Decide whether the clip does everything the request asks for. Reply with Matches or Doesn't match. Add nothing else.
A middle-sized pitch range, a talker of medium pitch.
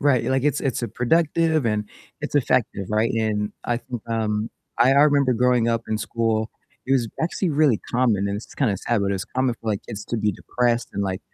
Doesn't match